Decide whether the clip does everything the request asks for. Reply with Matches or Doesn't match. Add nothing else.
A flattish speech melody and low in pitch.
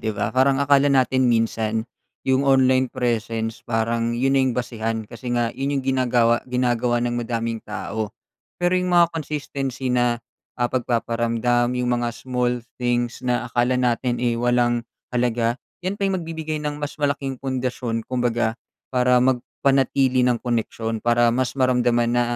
Matches